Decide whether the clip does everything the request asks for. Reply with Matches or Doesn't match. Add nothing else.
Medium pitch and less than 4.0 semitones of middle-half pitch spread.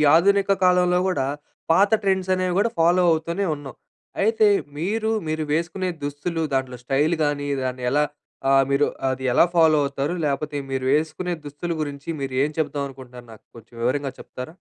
Doesn't match